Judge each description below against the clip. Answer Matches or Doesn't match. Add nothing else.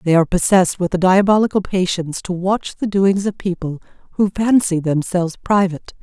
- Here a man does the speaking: Doesn't match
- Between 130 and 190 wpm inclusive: Matches